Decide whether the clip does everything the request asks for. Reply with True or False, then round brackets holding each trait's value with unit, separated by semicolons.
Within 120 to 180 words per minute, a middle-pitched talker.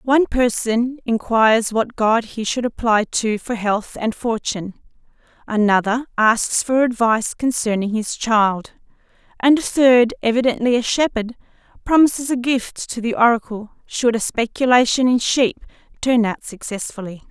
False (140 wpm; 230 Hz)